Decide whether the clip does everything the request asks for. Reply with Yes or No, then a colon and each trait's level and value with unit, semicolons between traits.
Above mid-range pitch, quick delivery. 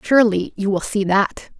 No: high, 205 Hz; average, 190 wpm